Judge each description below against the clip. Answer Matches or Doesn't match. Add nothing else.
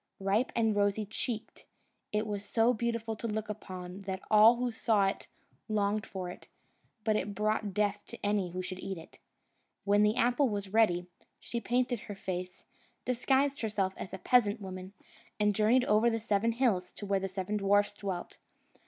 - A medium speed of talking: Matches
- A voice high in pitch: Matches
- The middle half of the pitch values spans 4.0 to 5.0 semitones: Doesn't match